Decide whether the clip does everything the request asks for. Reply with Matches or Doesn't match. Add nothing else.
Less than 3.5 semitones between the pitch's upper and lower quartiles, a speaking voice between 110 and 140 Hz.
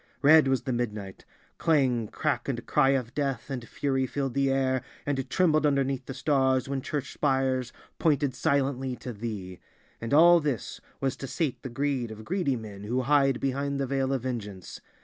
Matches